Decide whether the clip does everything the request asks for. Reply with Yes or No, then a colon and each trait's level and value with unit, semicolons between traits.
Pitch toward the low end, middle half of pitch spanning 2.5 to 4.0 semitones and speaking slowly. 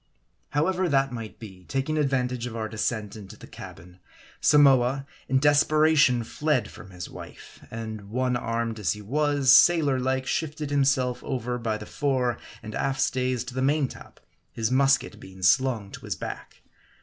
No: low, 130 Hz; average, 3.7 semitones; average, 165 wpm